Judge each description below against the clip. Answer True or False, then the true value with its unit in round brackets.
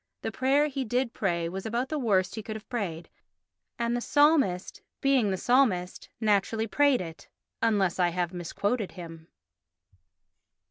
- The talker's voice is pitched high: True (215 Hz)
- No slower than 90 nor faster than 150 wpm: True (145 wpm)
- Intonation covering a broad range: True (5.7 semitones)